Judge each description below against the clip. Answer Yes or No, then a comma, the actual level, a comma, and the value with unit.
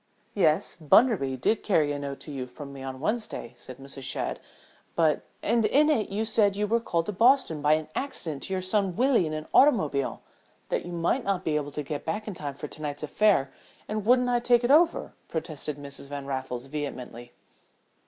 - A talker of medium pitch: Yes, medium, 160 Hz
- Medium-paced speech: No, fast, 210 wpm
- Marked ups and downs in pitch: Yes, wide, 7.2 semitones